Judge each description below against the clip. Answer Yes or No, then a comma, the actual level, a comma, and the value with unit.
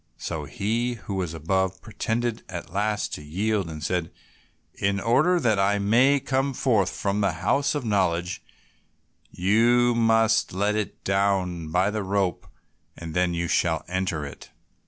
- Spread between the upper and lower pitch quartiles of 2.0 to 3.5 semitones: No, average, 4.1 semitones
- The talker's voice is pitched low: Yes, low, 100 Hz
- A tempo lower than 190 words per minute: Yes, average, 155 wpm